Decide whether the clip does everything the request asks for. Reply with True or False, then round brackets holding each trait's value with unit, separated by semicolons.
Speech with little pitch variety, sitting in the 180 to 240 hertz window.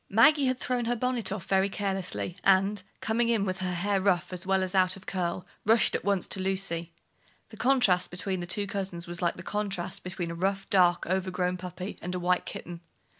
True (2.1 semitones; 190 Hz)